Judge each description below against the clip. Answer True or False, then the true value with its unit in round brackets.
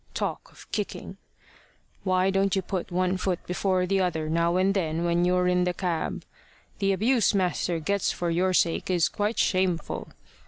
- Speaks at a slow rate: False (170 wpm)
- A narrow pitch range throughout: True (1.9 semitones)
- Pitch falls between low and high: True (180 Hz)